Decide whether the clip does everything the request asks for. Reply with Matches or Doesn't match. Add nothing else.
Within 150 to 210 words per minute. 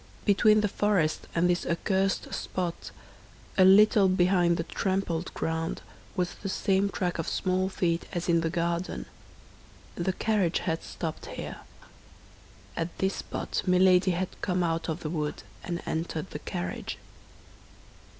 Doesn't match